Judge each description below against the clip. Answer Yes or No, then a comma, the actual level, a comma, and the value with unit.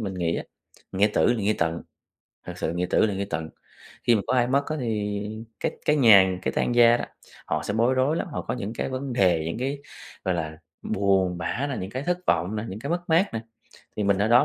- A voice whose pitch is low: Yes, low, 105 Hz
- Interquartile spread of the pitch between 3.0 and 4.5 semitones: No, wide, 5.4 semitones